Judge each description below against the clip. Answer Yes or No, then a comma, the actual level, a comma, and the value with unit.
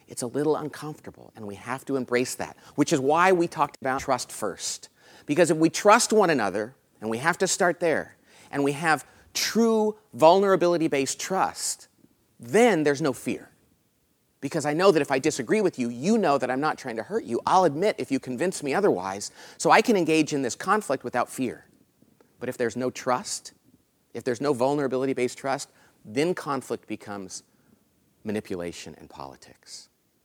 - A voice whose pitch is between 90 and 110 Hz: No, medium, 140 Hz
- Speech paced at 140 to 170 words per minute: No, average, 185 wpm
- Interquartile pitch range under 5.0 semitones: No, average, 5.3 semitones